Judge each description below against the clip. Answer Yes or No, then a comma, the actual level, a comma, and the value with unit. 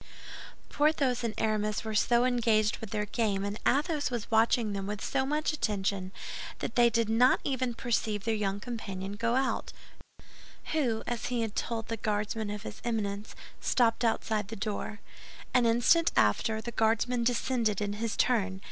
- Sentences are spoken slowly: No, average, 165 wpm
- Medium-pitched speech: No, high, 225 Hz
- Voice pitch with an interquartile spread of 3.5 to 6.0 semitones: No, average, 2.7 semitones